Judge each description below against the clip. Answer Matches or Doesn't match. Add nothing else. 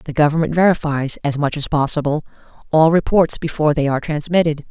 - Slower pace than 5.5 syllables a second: Doesn't match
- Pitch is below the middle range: Doesn't match